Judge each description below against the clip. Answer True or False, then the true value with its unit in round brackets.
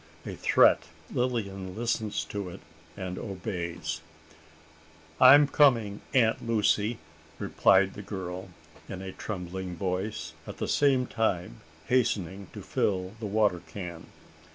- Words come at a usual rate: False (125 wpm)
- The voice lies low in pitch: True (100 Hz)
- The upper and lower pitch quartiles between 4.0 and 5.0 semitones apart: False (3.5 semitones)